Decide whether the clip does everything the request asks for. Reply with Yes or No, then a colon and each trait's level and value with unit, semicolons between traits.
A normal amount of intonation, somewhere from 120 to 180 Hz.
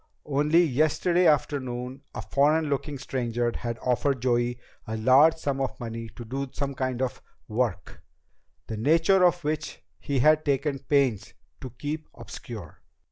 Yes: average, 3.7 semitones; low, 135 Hz